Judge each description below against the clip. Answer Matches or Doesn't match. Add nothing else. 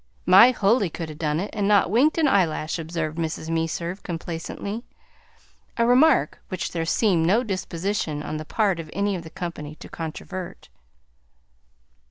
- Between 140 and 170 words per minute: Matches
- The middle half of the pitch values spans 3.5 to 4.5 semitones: Matches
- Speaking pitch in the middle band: Matches